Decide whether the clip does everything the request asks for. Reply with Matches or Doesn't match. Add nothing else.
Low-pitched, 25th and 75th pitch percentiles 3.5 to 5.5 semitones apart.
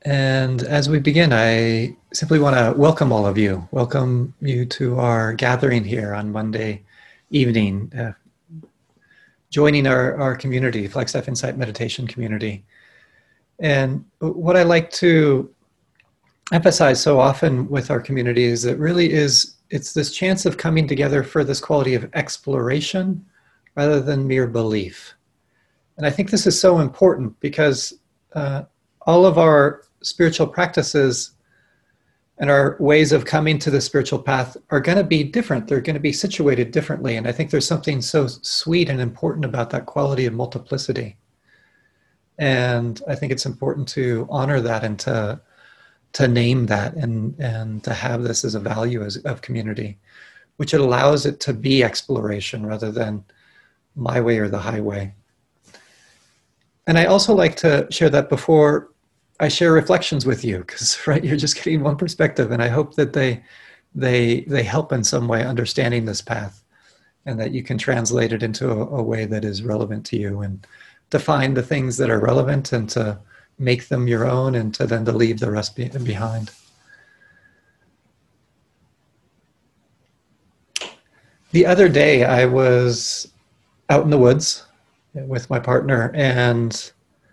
Matches